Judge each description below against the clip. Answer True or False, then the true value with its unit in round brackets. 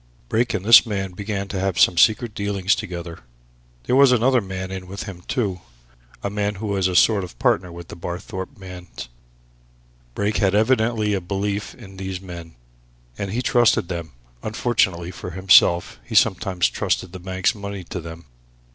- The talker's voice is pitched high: False (95 Hz)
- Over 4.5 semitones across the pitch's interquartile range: False (2.7 semitones)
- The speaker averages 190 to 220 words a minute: False (175 wpm)